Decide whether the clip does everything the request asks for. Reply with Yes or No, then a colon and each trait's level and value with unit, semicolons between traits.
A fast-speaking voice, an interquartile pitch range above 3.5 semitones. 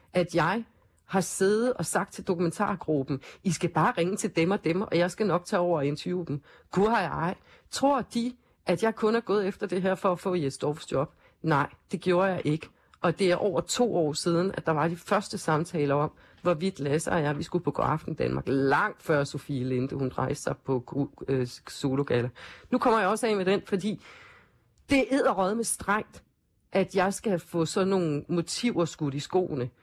No: average, 215 wpm; average, 4.9 semitones